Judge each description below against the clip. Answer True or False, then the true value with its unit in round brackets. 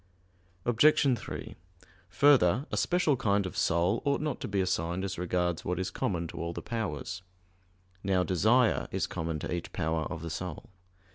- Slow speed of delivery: False (170 wpm)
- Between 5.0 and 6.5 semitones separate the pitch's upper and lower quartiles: True (5.3 semitones)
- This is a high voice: False (95 Hz)